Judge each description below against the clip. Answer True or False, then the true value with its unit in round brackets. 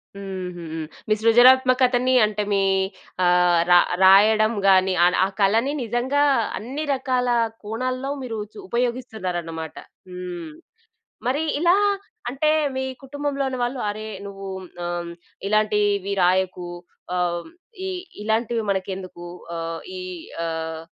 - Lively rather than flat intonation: True (5.7 semitones)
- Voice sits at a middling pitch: False (215 Hz)